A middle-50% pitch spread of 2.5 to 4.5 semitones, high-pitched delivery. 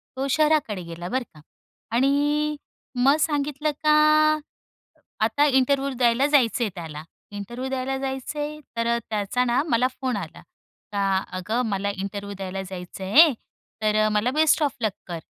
No: wide, 5.4 semitones; high, 245 Hz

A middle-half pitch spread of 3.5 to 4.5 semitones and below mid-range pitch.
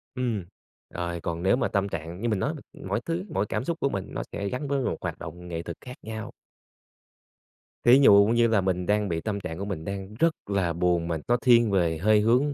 No: wide, 5.4 semitones; low, 100 Hz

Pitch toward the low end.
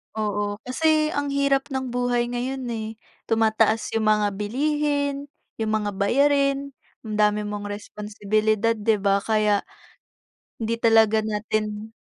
No: high, 220 Hz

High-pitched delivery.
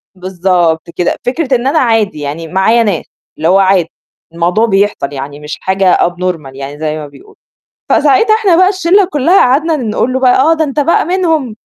Yes: high, 215 Hz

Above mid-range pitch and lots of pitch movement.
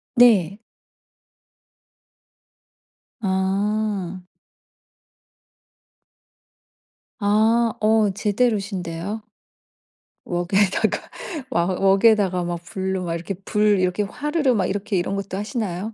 No: high, 200 Hz; average, 2.8 semitones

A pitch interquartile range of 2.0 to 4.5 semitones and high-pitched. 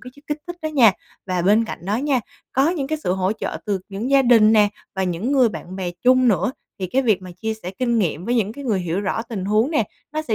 No: average, 5.2 semitones; high, 220 Hz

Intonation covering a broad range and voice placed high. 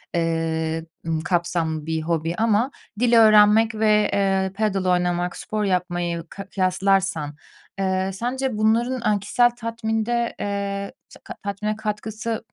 No: average, 3.8 semitones; high, 200 Hz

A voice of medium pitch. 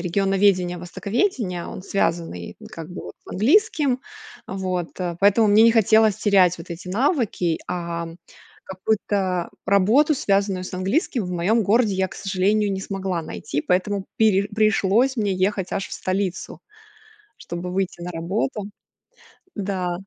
No: high, 195 Hz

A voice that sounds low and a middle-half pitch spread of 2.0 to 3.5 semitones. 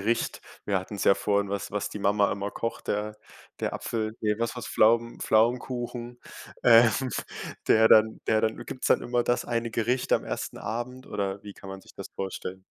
Yes: low, 110 Hz; narrow, 2.6 semitones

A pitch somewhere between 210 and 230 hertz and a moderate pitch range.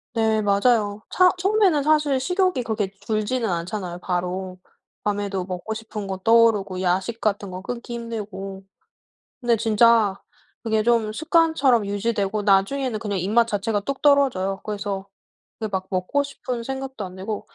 Yes: high, 215 Hz; average, 3.7 semitones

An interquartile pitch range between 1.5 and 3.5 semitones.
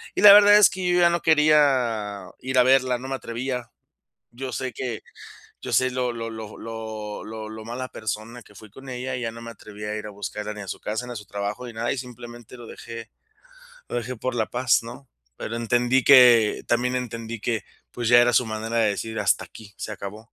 Yes: average, 2.7 semitones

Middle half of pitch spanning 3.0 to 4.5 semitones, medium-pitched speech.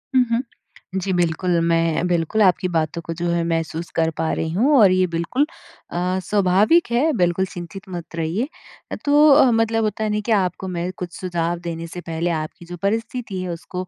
Yes: average, 3.9 semitones; medium, 180 Hz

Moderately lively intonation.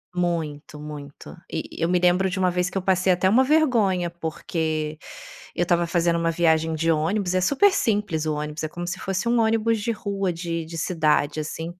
Yes: average, 3.1 semitones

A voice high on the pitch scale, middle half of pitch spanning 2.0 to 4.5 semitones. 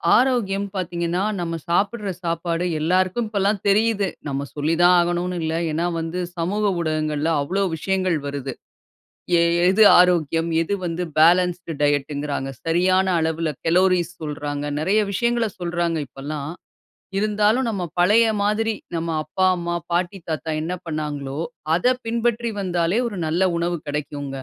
No: medium, 175 Hz; average, 3.7 semitones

